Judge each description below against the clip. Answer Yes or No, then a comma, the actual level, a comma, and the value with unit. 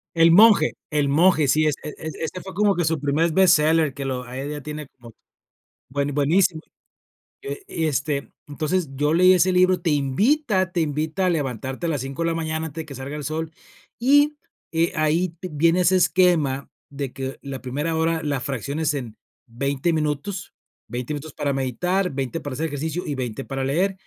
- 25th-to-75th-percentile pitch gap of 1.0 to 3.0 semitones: No, average, 3.8 semitones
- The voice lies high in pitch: No, medium, 155 Hz